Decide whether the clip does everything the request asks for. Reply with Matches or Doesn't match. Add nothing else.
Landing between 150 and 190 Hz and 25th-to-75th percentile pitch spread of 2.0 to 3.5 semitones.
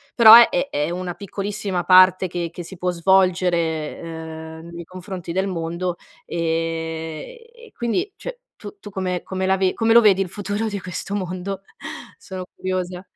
Matches